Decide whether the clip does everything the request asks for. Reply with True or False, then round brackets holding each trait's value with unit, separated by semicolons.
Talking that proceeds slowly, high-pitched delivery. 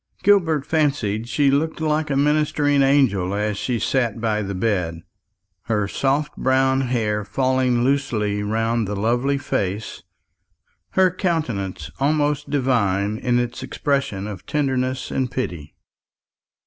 False (125 wpm; 125 Hz)